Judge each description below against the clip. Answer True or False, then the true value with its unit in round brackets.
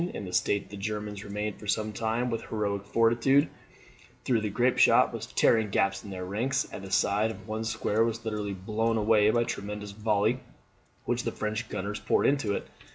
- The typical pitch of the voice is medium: False (105 Hz)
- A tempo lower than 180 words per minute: False (200 wpm)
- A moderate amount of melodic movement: False (1.9 semitones)